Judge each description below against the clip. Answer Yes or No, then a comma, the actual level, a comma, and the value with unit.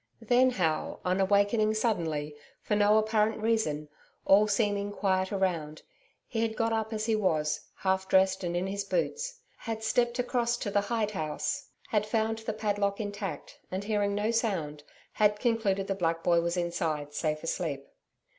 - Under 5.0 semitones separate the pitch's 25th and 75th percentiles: Yes, average, 3.8 semitones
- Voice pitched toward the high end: Yes, high, 205 Hz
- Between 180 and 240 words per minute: No, average, 165 wpm